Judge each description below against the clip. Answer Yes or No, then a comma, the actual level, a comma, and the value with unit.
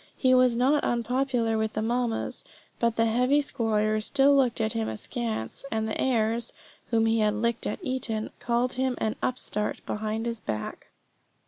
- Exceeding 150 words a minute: Yes, average, 165 wpm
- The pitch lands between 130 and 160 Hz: No, high, 230 Hz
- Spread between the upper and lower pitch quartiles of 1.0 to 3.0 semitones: Yes, narrow, 2.6 semitones